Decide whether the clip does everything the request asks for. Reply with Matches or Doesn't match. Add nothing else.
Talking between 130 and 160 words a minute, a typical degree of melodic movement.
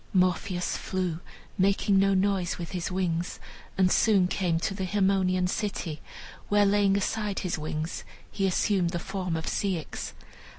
Doesn't match